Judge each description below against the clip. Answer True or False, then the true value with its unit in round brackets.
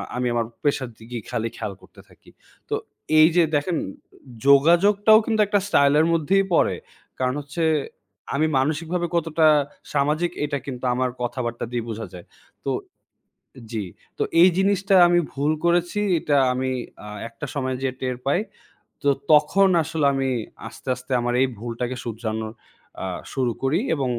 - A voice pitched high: False (140 Hz)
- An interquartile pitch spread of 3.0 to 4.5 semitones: False (5.2 semitones)